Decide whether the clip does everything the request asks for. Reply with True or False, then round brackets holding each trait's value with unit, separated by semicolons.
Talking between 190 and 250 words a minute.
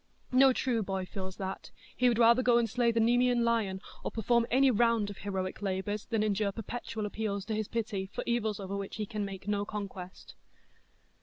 True (200 wpm)